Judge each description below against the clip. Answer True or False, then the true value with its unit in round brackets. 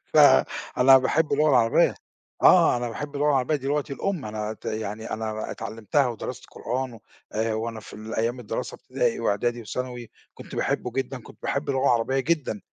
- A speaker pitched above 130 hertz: False (125 Hz)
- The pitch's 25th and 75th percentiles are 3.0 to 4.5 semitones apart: True (3.5 semitones)